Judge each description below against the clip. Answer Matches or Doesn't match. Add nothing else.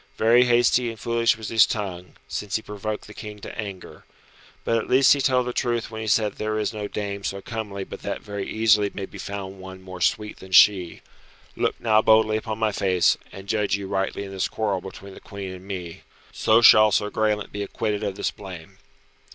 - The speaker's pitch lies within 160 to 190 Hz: Doesn't match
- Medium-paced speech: Doesn't match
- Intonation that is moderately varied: Doesn't match